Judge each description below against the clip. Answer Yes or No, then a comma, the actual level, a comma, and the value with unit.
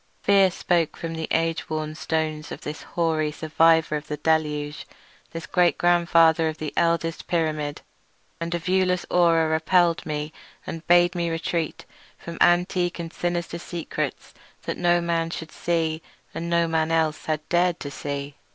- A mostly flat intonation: Yes, narrow, 1.6 semitones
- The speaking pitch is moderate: Yes, medium, 165 Hz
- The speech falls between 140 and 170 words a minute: Yes, average, 160 wpm